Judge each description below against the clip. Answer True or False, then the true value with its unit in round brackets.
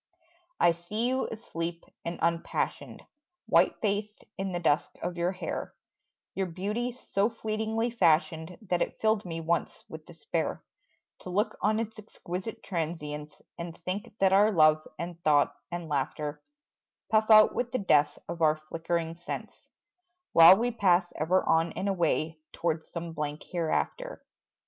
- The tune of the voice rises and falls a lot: False (4.4 semitones)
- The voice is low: False (175 Hz)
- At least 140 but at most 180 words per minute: True (150 wpm)